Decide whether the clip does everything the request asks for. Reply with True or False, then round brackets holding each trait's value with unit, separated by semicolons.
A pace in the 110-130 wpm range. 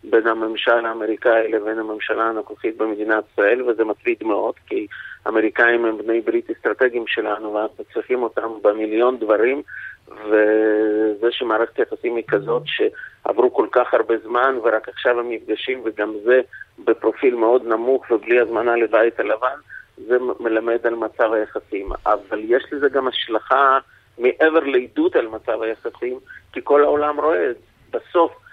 False (140 wpm)